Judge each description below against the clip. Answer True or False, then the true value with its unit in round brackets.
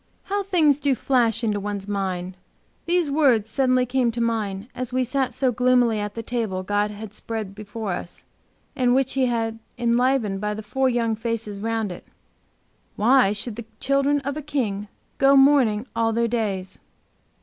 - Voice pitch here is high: True (230 Hz)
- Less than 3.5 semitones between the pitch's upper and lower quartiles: False (3.9 semitones)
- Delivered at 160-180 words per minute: True (170 wpm)